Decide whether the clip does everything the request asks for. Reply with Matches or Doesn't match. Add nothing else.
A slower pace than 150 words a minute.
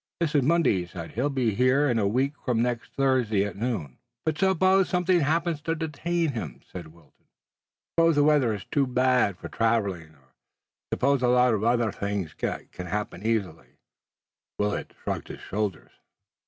Doesn't match